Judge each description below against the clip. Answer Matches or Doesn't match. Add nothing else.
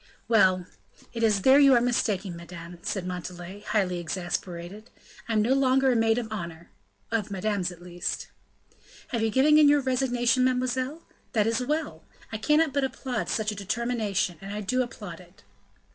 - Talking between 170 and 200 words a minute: Matches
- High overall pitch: Matches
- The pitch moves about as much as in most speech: Doesn't match